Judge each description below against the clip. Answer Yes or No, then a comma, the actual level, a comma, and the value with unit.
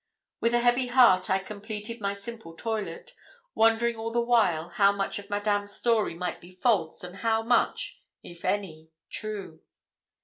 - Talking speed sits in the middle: Yes, average, 160 wpm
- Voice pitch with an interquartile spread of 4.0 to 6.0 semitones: No, average, 3.6 semitones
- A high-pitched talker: Yes, high, 210 Hz